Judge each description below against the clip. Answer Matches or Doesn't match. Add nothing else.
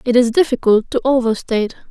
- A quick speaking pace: Doesn't match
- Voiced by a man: Doesn't match